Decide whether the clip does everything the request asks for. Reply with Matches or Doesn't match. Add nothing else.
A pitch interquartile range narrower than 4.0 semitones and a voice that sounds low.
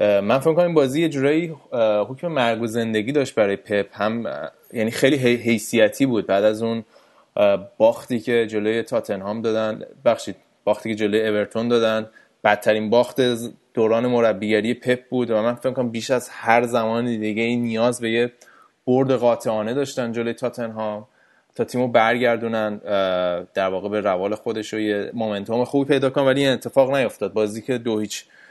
Matches